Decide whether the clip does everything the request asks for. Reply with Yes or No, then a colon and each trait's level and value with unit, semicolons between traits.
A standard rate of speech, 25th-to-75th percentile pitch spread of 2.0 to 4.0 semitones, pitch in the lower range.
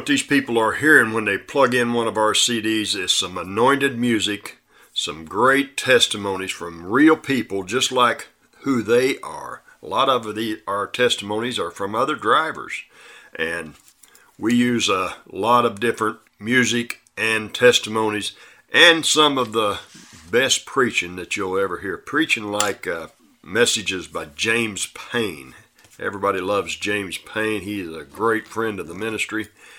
Yes: average, 155 wpm; average, 3.1 semitones; low, 110 Hz